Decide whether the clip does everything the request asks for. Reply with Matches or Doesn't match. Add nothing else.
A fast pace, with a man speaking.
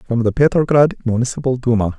Doesn't match